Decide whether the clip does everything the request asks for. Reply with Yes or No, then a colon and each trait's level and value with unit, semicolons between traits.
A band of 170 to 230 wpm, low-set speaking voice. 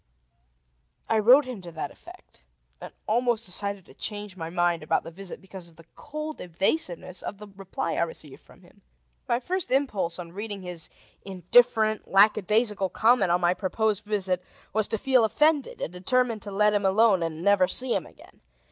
No: average, 180 wpm; high, 200 Hz